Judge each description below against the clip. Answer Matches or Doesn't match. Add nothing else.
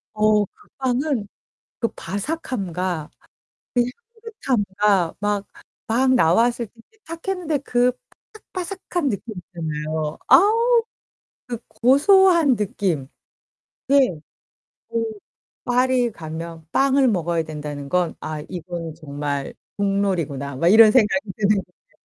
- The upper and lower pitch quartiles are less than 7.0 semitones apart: Doesn't match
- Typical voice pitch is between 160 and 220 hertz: Matches